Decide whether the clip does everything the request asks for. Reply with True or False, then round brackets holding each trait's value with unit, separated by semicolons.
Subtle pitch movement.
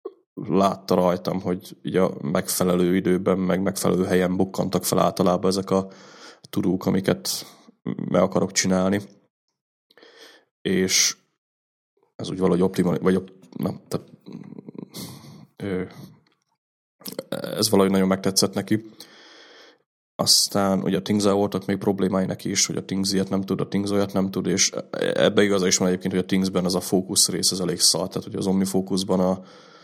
True (1.1 semitones)